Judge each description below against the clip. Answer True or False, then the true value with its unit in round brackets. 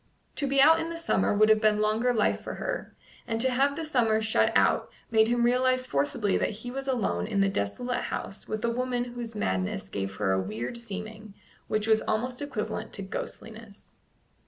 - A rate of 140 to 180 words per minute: False (200 wpm)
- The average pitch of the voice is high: True (220 Hz)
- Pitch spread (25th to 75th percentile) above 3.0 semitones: True (3.5 semitones)